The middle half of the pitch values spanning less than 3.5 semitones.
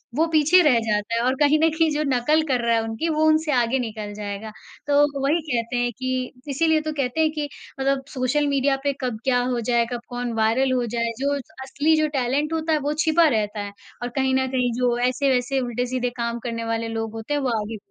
No: average, 3.9 semitones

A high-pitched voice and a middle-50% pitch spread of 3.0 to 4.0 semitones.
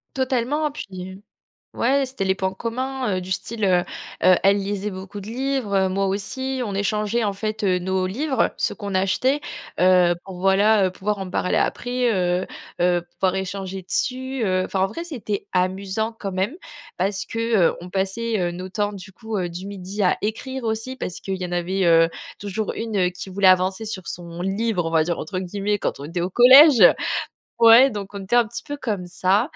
Yes: high, 200 Hz; average, 3.6 semitones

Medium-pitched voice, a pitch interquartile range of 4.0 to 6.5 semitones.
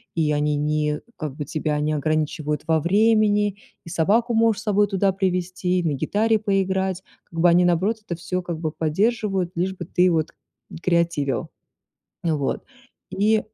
Yes: medium, 180 Hz; average, 4.3 semitones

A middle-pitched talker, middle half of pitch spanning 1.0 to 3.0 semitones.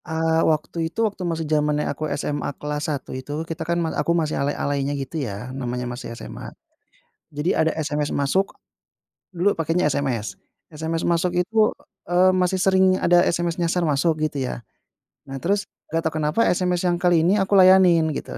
No: medium, 165 Hz; average, 3.5 semitones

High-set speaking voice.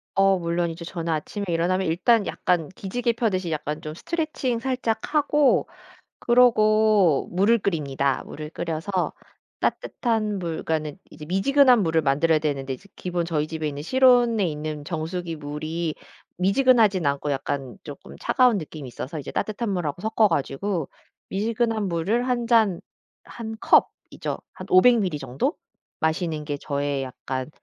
No: medium, 175 Hz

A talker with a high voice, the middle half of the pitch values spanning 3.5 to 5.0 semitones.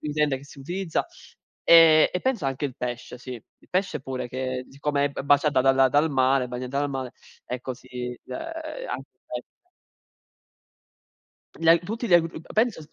No: medium, 140 Hz; average, 4.4 semitones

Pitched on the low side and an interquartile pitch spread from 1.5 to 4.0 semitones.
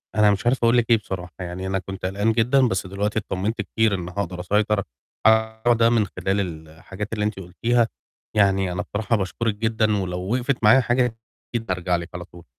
Yes: low, 105 Hz; average, 3.3 semitones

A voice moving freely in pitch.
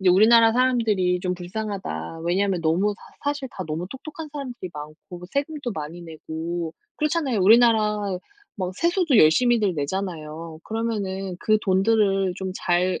No: average, 4.8 semitones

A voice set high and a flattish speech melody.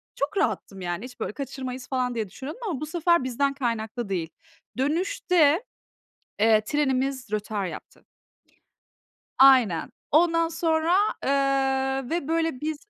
No: very high, 270 Hz; average, 4.7 semitones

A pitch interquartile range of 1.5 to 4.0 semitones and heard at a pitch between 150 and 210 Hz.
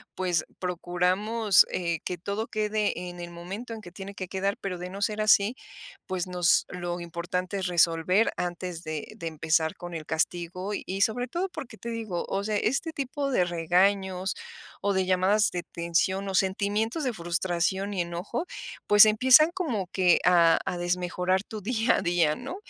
Yes: average, 3.3 semitones; medium, 185 Hz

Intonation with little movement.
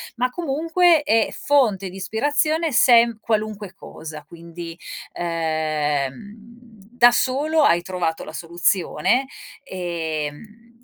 No: wide, 6.7 semitones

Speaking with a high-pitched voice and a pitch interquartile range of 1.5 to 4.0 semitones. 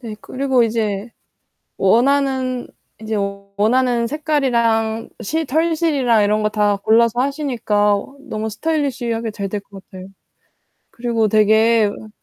Yes: high, 230 Hz; average, 3.6 semitones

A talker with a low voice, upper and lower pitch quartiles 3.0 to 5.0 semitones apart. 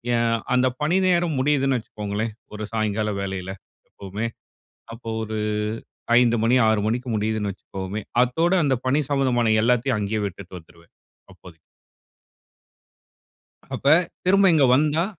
Yes: low, 115 Hz; average, 4.7 semitones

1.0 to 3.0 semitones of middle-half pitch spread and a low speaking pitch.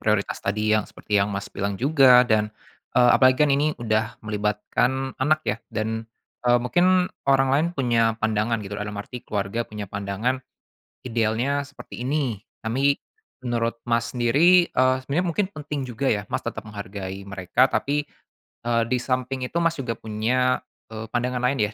No: average, 3.8 semitones; low, 120 Hz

